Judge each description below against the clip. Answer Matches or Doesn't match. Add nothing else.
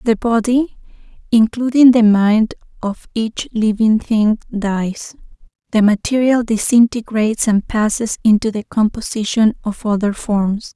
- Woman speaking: Matches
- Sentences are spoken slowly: Matches